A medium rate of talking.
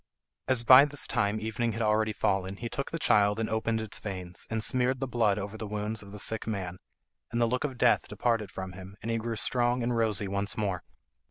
No: fast, 230 wpm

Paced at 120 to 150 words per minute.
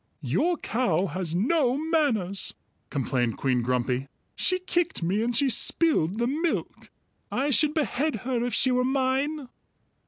Yes: average, 145 wpm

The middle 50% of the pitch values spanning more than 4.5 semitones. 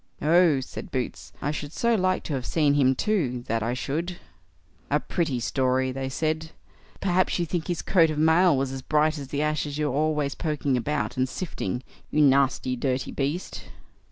No: average, 3.5 semitones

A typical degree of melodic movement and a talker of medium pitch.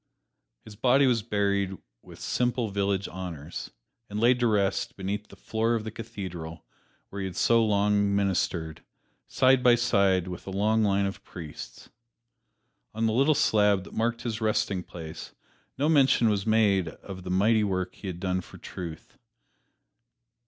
No: average, 3.2 semitones; low, 100 Hz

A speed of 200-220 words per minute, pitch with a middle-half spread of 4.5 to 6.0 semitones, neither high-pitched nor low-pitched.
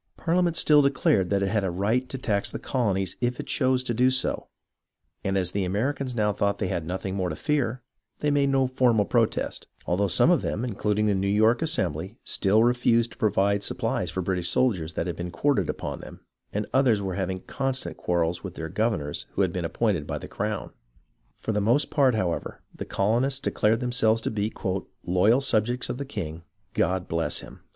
No: fast, 205 wpm; average, 5.1 semitones; low, 105 Hz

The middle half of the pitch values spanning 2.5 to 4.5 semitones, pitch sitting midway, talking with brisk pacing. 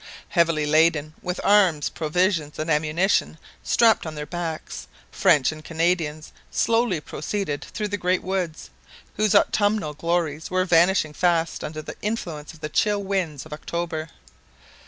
No: average, 3.5 semitones; medium, 165 Hz; average, 140 wpm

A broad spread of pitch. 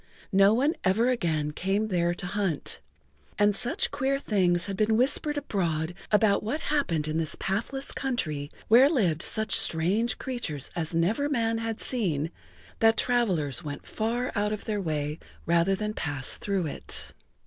Yes: wide, 5.8 semitones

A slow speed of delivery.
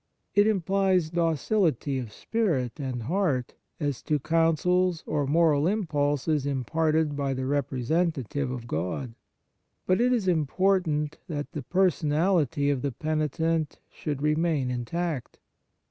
Yes: slow, 130 wpm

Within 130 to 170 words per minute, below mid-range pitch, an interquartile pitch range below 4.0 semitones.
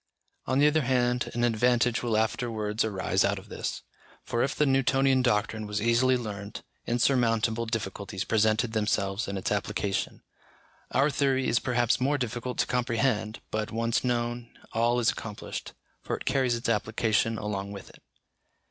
Yes: average, 155 wpm; low, 115 Hz; narrow, 2.5 semitones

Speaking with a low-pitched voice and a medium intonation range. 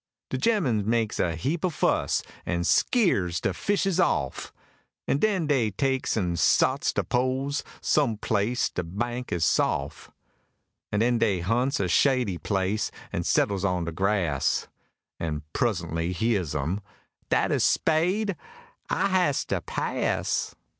No: low, 110 Hz; wide, 7.4 semitones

